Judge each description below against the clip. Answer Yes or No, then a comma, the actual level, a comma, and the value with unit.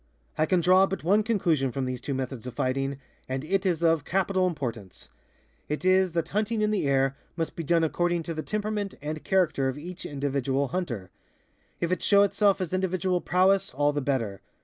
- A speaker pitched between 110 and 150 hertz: No, medium, 165 Hz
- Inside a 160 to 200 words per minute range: Yes, average, 195 wpm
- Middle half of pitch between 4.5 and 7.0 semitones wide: Yes, wide, 5.5 semitones